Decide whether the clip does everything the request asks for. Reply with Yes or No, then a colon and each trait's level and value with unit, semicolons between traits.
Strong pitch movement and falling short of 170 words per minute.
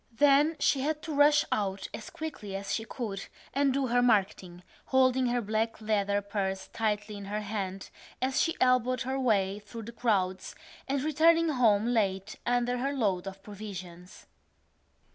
No: average, 4.7 semitones; average, 160 wpm